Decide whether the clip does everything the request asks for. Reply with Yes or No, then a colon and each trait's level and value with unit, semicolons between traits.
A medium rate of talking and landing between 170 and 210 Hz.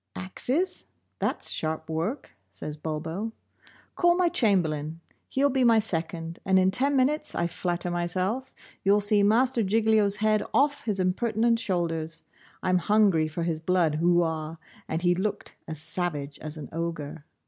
Yes: average, 150 wpm; medium, 185 Hz